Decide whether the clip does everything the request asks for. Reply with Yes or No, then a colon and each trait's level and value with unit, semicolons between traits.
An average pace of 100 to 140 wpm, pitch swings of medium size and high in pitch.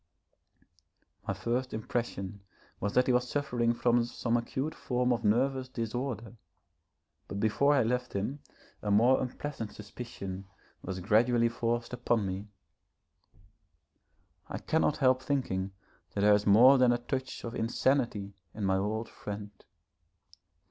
No: slow, 135 wpm; average, 3.4 semitones; low, 120 Hz